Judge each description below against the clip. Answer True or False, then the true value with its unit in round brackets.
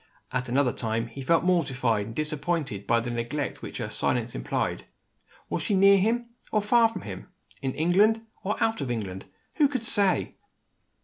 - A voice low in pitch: False (150 Hz)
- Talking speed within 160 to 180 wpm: True (175 wpm)